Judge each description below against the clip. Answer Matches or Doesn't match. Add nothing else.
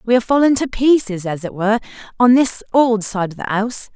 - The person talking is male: Doesn't match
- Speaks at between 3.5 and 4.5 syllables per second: Doesn't match